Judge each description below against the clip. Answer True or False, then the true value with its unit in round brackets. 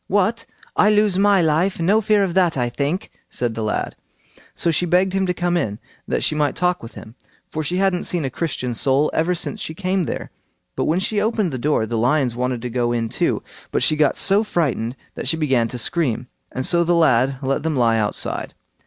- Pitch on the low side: False (160 Hz)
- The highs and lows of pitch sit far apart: True (6.6 semitones)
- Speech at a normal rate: False (225 wpm)